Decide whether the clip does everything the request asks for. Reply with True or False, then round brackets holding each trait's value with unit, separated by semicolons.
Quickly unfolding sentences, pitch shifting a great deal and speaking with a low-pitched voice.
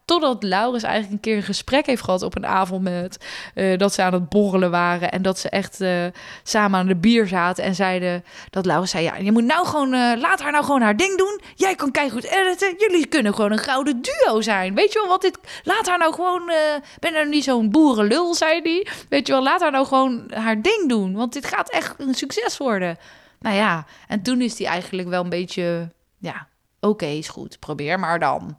False (235 wpm; 8.3 semitones; 230 Hz)